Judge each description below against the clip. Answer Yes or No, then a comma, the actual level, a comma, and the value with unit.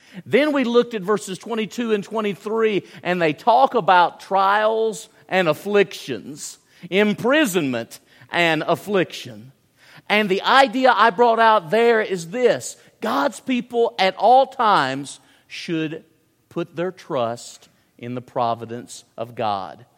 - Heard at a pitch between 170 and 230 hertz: Yes, high, 190 Hz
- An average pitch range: No, wide, 6.1 semitones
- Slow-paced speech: Yes, slow, 125 wpm